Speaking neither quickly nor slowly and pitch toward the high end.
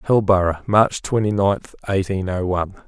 No: average, 145 wpm; very low, 95 Hz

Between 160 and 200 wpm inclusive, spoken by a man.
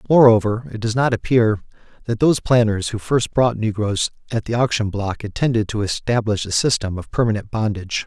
Yes: average, 180 wpm; male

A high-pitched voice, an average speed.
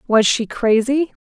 Yes: high, 245 Hz; average, 145 wpm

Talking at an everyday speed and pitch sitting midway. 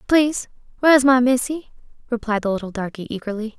No: average, 165 wpm; high, 240 Hz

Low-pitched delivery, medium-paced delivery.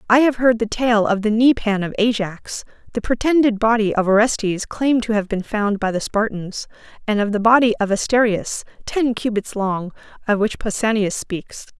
No: high, 215 Hz; average, 185 wpm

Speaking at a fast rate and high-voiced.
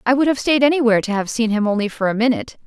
Yes: fast, 290 wpm; high, 235 Hz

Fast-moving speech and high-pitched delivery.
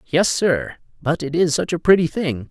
No: fast, 215 wpm; medium, 155 Hz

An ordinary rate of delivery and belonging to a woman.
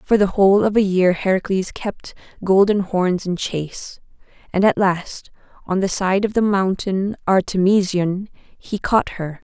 Yes: average, 160 wpm; female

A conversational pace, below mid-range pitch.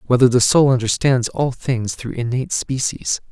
Yes: average, 165 wpm; low, 125 Hz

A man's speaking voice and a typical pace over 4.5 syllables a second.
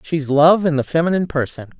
No: female; 6.1 syllables/s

